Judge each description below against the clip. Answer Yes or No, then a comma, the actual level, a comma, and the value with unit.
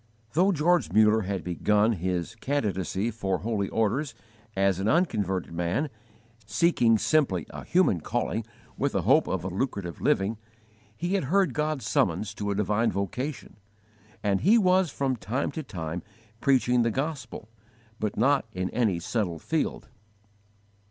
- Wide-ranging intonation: Yes, wide, 6.4 semitones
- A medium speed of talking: Yes, average, 145 wpm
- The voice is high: No, low, 110 Hz